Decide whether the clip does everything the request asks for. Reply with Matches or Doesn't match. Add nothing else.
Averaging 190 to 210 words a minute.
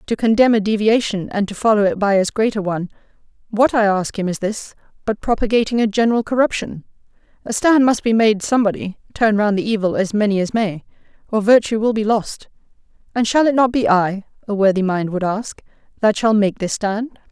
Matches